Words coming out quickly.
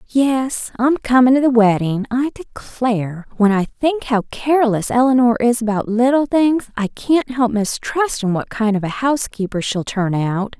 No: average, 165 wpm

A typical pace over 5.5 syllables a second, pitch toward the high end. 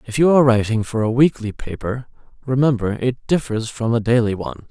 No: 5.9 syllables/s; low, 120 Hz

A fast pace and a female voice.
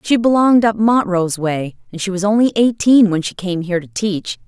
Yes: fast, 215 wpm; female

